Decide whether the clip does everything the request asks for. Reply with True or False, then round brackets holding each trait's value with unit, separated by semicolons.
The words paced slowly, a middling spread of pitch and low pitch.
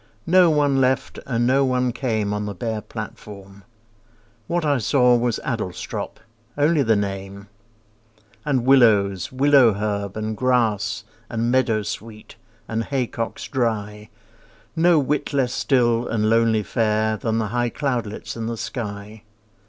True (130 wpm; 3.5 semitones; 115 Hz)